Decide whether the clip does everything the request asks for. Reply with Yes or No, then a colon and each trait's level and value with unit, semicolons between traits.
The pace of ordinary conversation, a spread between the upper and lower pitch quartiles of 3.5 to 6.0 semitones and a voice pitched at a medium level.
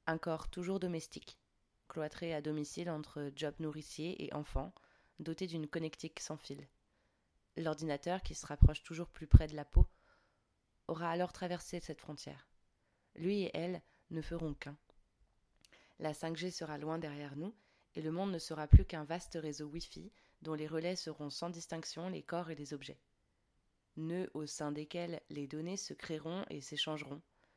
No: average, 165 wpm; narrow, 2.4 semitones; medium, 155 Hz